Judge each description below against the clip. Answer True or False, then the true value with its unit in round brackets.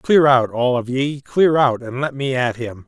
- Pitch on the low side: True (130 Hz)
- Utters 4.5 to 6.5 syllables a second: False (4.2 syllables/s)